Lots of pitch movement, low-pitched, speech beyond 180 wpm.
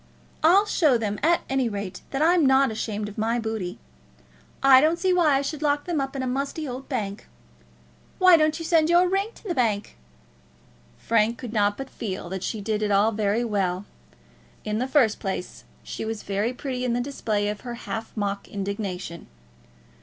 No: wide, 5.8 semitones; high, 240 Hz; average, 190 wpm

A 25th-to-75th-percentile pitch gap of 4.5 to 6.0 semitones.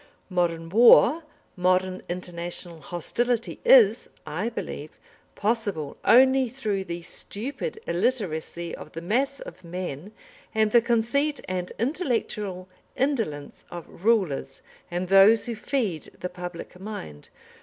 Yes: wide, 5.4 semitones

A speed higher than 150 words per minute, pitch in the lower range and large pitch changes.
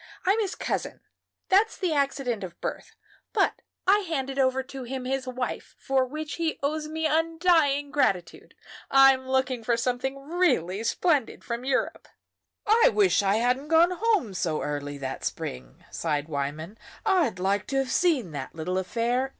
No: average, 160 wpm; very high, 265 Hz; wide, 7.4 semitones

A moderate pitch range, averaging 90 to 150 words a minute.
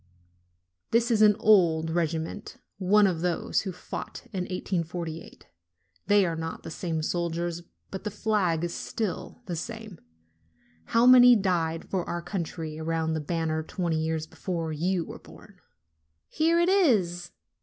Yes: average, 4.1 semitones; average, 145 wpm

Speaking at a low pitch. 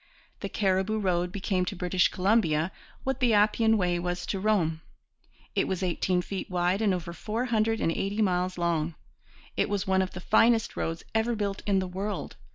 No: high, 190 Hz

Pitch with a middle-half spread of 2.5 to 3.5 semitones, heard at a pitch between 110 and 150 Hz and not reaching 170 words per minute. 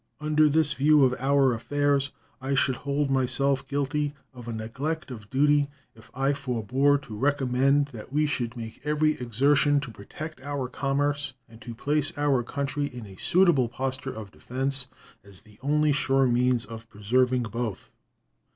Yes: average, 2.9 semitones; low, 135 Hz; average, 160 wpm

